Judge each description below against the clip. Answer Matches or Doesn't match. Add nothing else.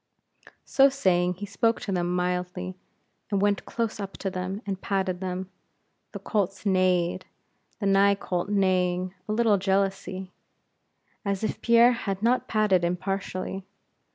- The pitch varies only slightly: Matches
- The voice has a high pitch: Matches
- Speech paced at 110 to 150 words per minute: Matches